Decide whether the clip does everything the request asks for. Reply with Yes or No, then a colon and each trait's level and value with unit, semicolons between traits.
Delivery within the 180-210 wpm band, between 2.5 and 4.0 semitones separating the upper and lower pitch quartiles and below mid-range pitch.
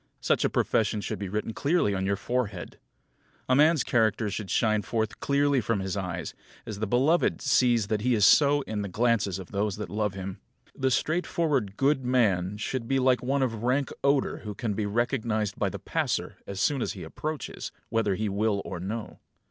No: average, 200 wpm; average, 4.4 semitones; low, 110 Hz